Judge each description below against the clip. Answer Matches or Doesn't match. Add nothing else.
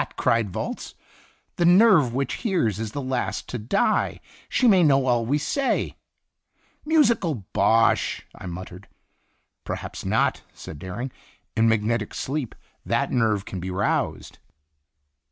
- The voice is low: Matches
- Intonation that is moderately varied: Doesn't match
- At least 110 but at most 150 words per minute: Matches